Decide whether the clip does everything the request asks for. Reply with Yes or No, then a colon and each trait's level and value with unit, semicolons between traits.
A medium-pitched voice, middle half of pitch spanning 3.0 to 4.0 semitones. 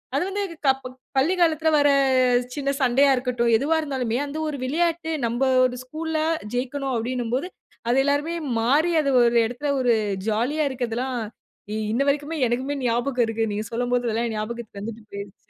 No: very high, 255 Hz; average, 3.4 semitones